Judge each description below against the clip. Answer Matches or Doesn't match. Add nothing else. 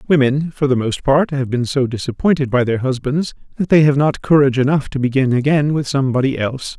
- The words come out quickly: Matches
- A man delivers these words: Matches